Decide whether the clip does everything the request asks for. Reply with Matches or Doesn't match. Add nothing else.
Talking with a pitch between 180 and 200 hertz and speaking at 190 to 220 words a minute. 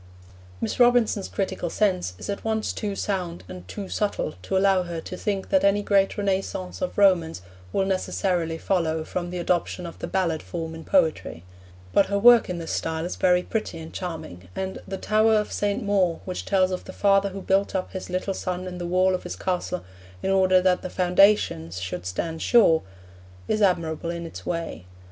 Matches